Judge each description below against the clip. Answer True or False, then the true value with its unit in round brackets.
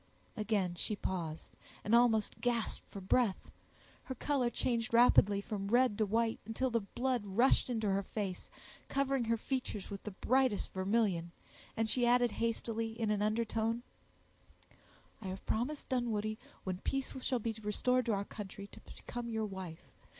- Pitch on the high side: True (225 Hz)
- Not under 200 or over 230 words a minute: False (155 wpm)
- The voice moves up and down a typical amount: True (3.2 semitones)